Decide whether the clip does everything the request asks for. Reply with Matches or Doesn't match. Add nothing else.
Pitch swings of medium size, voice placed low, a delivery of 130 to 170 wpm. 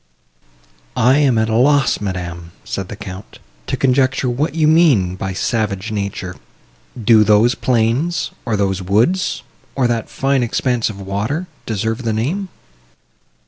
Matches